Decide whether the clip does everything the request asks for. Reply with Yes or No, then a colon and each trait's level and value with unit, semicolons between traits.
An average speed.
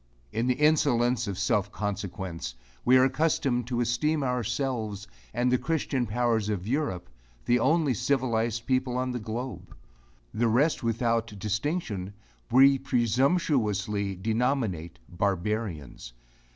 No: slow, 120 wpm